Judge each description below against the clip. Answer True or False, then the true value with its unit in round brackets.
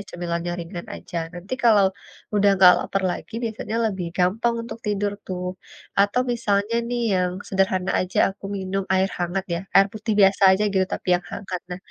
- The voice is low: False (195 Hz)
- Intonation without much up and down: True (2.2 semitones)